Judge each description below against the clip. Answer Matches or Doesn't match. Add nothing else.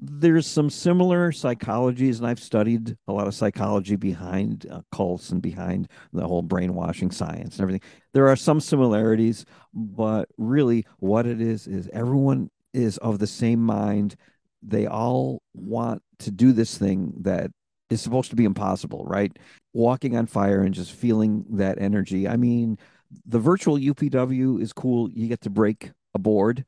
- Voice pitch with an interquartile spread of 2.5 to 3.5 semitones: Doesn't match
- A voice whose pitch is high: Doesn't match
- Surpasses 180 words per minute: Doesn't match